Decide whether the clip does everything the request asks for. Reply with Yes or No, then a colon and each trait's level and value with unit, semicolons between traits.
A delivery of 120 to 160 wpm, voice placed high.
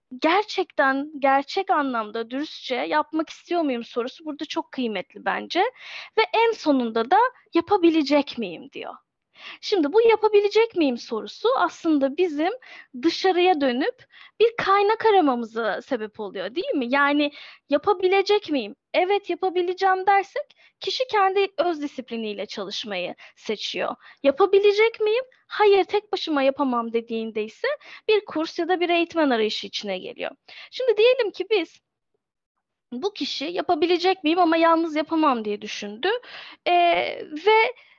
Yes: average, 125 wpm; very high, 325 Hz